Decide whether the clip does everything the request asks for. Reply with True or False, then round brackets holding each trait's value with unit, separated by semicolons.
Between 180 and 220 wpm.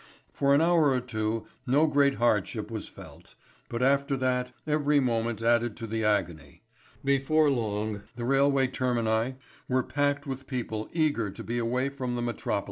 False (165 wpm)